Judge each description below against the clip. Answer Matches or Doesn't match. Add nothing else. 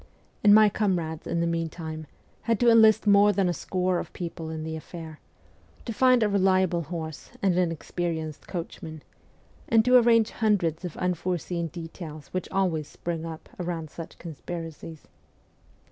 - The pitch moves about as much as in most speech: Matches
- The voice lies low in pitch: Doesn't match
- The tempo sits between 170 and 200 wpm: Doesn't match